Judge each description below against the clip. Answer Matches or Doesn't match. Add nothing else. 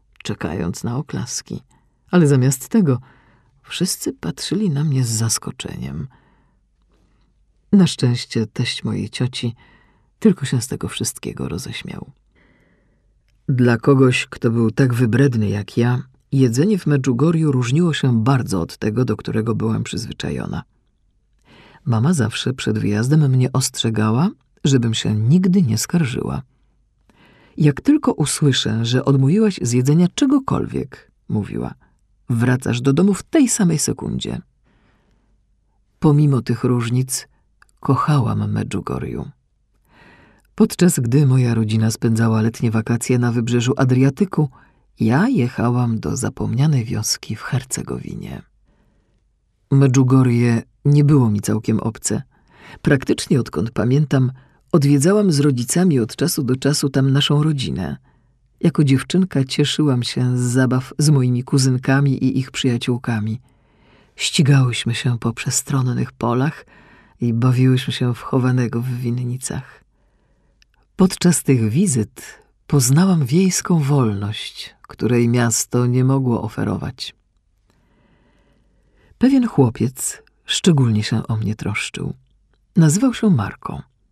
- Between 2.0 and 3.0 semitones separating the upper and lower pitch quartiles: Doesn't match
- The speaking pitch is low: Matches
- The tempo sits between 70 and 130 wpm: Matches